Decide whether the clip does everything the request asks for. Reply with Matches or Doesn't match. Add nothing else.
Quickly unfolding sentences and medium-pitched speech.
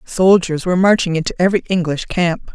Doesn't match